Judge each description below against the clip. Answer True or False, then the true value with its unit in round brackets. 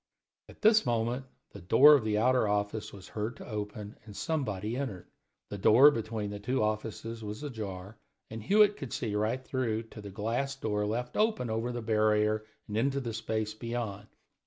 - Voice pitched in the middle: False (110 Hz)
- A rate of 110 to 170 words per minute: False (180 wpm)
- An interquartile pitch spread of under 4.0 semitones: True (3.0 semitones)